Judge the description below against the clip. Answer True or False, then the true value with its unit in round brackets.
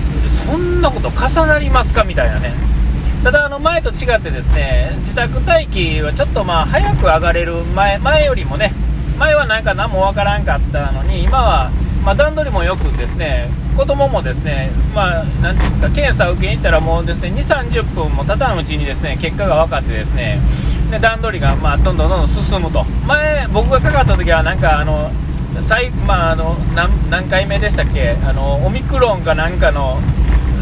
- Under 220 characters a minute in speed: False (365 characters per minute)